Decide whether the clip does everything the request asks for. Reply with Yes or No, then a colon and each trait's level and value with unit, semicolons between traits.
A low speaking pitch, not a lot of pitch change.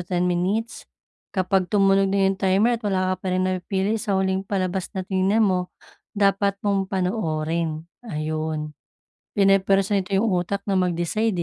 No: high, 190 Hz; narrow, 1.7 semitones